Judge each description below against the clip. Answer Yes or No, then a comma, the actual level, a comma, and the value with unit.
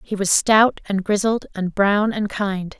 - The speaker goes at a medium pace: Yes, average, 195 wpm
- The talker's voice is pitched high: Yes, high, 200 Hz